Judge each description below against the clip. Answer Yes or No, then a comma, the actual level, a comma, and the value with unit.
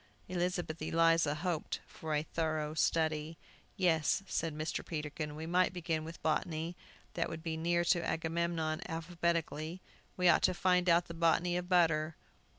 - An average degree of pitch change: No, narrow, 1.7 semitones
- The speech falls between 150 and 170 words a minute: Yes, average, 155 wpm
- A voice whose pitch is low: No, medium, 165 Hz